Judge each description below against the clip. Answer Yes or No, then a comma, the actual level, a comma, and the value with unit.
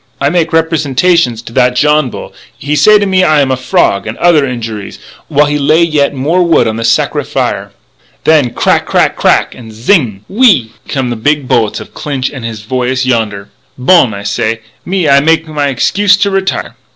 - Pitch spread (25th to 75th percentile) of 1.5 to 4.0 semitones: No, wide, 5.5 semitones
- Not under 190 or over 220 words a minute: Yes, average, 200 wpm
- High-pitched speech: No, medium, 140 Hz